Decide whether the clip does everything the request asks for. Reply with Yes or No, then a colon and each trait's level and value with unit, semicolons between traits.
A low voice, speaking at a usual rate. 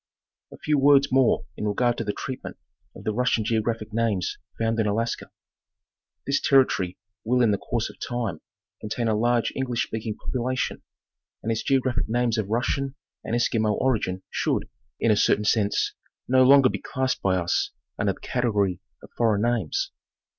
Yes: low, 115 Hz; average, 170 wpm